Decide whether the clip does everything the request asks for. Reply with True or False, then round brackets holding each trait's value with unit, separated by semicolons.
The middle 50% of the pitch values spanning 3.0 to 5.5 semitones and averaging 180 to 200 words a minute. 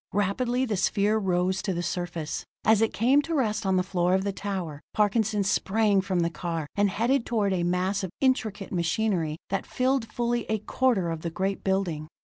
True (3.4 semitones; 195 wpm)